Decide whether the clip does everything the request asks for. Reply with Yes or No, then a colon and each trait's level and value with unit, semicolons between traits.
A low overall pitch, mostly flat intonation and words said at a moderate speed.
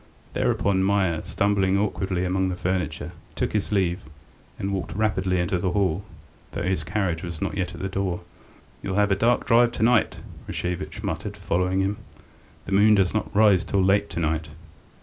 Yes: very low, 95 Hz; narrow, 2.2 semitones; average, 180 wpm